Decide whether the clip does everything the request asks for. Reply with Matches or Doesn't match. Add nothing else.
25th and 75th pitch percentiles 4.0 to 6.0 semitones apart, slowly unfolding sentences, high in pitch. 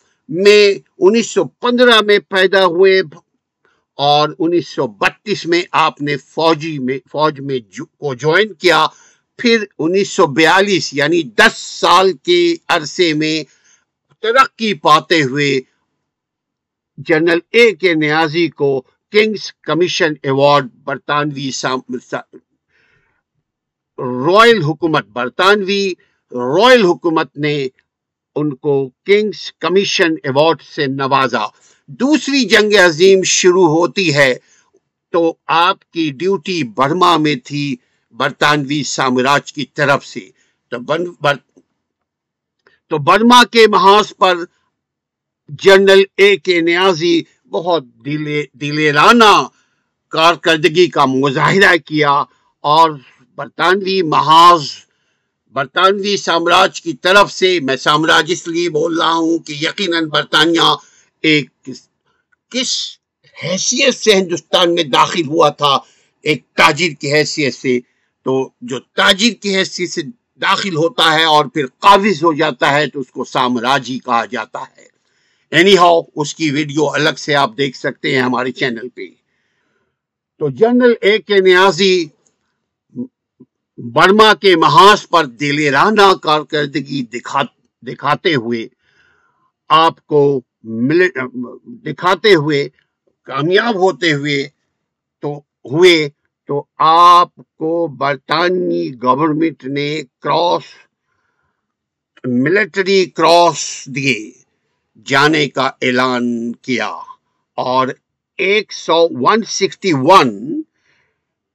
Doesn't match